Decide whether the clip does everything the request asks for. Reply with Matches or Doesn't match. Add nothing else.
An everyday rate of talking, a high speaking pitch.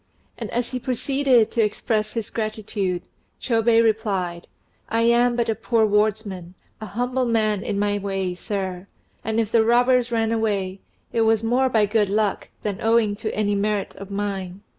Matches